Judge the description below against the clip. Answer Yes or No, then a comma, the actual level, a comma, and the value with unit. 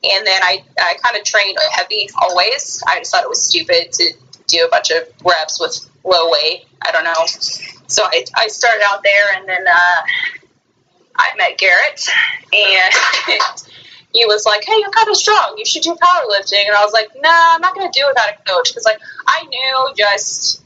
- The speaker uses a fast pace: Yes, fast, 210 wpm